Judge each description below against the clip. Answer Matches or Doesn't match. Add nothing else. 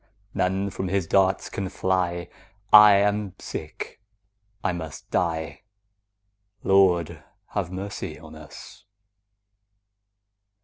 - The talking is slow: Matches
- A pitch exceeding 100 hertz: Doesn't match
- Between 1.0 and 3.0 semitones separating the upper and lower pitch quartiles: Matches